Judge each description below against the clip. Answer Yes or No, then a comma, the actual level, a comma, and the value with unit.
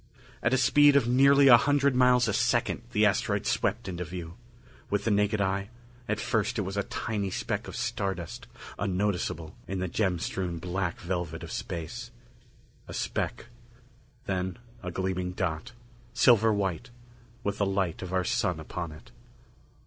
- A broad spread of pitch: No, average, 4.6 semitones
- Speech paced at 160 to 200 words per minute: Yes, average, 165 wpm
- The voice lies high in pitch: No, low, 100 Hz